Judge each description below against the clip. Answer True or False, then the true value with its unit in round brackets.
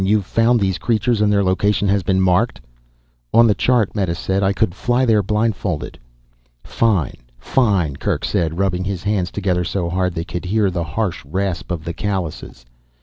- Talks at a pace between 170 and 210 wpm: True (180 wpm)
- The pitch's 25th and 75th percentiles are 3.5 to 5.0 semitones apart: False (3.1 semitones)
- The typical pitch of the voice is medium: False (95 Hz)